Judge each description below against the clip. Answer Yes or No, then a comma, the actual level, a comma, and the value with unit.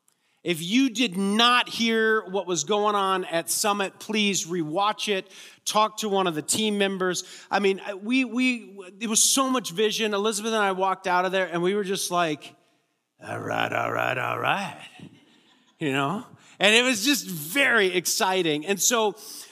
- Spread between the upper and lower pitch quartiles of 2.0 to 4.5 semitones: Yes, average, 3.0 semitones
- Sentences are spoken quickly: No, average, 180 wpm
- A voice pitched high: Yes, high, 200 Hz